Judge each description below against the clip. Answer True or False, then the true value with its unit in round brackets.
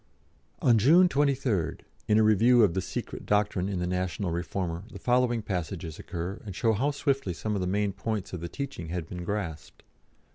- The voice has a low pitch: True (100 Hz)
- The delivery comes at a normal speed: True (190 wpm)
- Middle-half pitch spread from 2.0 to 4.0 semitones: False (4.8 semitones)